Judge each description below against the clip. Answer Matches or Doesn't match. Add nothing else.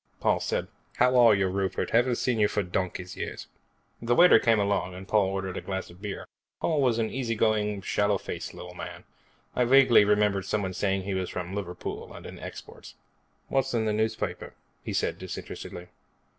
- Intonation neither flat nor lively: Matches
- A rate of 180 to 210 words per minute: Matches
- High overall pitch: Doesn't match